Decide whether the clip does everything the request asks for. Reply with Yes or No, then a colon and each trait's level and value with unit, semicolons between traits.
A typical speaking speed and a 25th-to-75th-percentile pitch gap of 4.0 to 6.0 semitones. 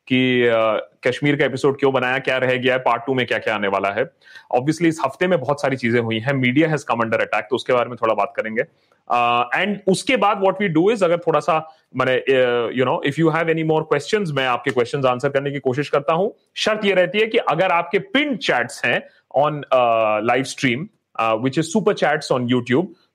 No: fast, 225 wpm; average, 4.9 semitones